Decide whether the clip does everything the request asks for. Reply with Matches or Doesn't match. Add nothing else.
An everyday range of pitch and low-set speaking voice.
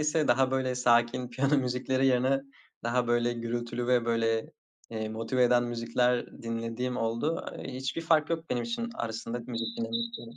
Doesn't match